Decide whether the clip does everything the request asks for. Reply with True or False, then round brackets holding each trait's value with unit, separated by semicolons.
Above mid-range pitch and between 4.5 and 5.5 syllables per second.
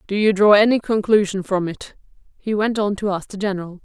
False (200 Hz; 5.8 syllables/s)